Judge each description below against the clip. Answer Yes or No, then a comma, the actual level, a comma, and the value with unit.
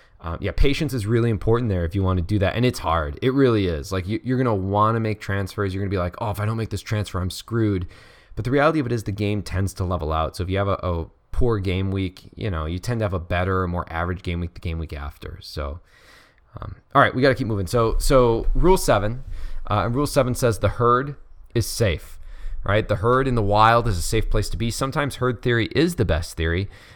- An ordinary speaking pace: No, fast, 270 wpm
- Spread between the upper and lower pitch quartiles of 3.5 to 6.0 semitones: Yes, average, 4.5 semitones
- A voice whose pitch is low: Yes, low, 105 Hz